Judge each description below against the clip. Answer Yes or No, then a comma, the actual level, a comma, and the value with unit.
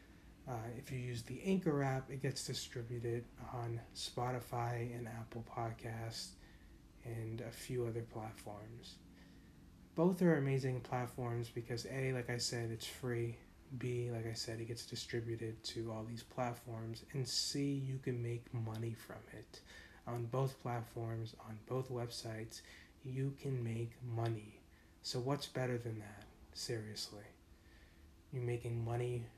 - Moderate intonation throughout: No, narrow, 1.9 semitones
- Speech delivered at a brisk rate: No, average, 140 wpm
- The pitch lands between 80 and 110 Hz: No, low, 120 Hz